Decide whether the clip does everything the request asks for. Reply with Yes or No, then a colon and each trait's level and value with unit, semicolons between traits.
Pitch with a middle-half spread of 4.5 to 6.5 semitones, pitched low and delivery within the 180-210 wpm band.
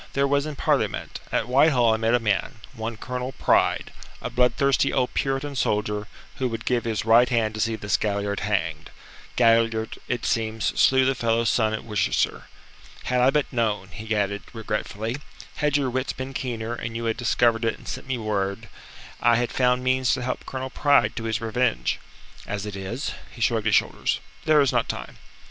No: average, 2.8 semitones; low, 115 Hz; average, 190 wpm